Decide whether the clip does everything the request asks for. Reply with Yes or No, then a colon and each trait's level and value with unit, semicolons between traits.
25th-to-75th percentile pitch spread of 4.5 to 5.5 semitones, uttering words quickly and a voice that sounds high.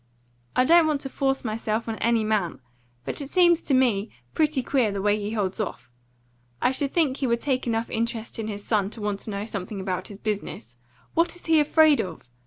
Yes: average, 5.0 semitones; fast, 215 wpm; high, 230 Hz